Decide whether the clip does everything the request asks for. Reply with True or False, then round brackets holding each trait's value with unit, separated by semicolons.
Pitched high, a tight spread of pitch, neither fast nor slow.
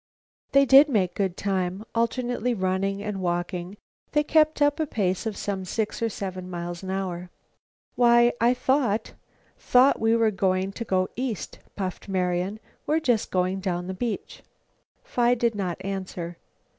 False (200 Hz; 4.4 semitones; 155 wpm)